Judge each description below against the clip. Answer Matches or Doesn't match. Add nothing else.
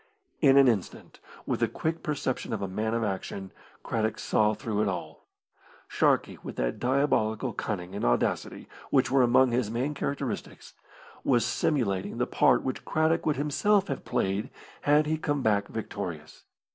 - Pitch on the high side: Doesn't match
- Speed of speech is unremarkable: Matches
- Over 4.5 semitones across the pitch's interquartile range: Matches